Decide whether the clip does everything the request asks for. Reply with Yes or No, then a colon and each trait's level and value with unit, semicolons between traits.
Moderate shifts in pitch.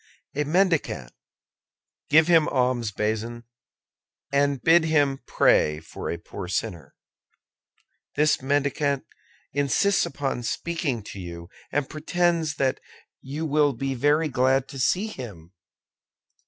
Yes: average, 4.5 semitones